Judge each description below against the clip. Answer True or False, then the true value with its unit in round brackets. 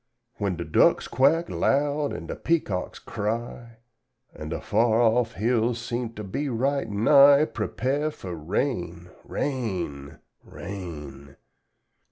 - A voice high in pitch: False (115 Hz)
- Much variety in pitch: True (6.9 semitones)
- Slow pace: True (120 wpm)